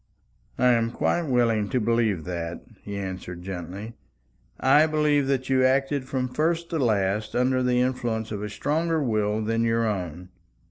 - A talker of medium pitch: No, low, 115 Hz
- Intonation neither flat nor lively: Yes, average, 4.4 semitones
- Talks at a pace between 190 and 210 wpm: No, average, 165 wpm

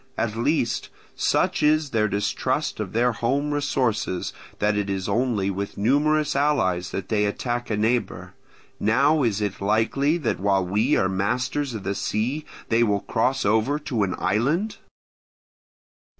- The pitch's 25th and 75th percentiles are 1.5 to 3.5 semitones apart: No, average, 5.3 semitones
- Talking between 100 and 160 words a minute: Yes, average, 150 wpm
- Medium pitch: No, low, 115 Hz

